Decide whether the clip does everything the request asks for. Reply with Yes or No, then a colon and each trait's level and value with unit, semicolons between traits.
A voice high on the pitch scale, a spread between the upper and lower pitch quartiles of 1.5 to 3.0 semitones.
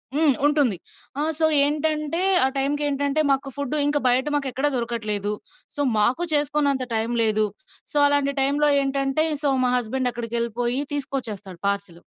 No: very high, 270 Hz; average, 3.7 semitones